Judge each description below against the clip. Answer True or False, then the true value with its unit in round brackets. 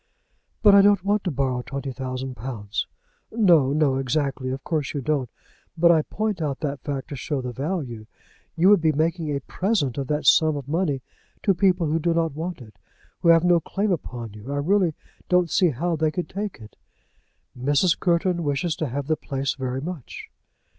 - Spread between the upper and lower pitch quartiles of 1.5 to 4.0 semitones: False (4.5 semitones)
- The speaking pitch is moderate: True (150 Hz)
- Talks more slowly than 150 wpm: False (195 wpm)